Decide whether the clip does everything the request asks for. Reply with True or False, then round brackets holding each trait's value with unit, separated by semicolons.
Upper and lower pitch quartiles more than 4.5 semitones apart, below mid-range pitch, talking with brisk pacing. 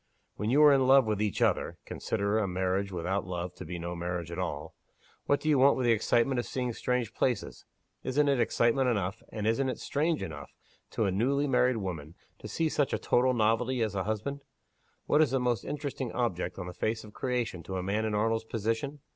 True (5.1 semitones; 115 Hz; 220 wpm)